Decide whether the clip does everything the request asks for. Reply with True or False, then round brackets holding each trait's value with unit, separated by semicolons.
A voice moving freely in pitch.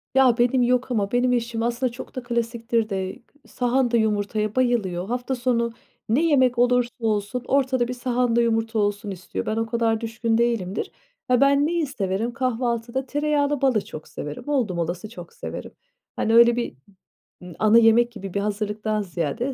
False (2.8 semitones)